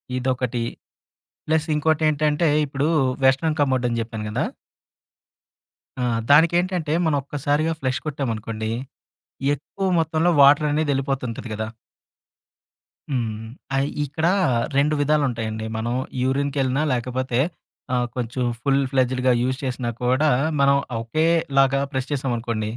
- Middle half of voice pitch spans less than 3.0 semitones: No, average, 3.4 semitones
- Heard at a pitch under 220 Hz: Yes, low, 135 Hz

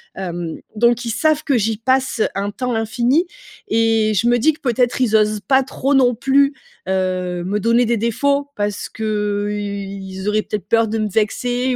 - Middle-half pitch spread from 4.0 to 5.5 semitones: No, average, 3.4 semitones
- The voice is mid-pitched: No, high, 225 Hz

